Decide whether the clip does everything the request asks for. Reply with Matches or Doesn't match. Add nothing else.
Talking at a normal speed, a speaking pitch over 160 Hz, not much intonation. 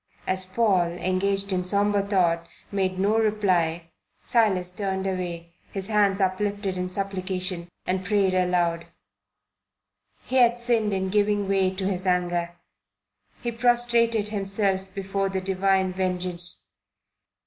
Doesn't match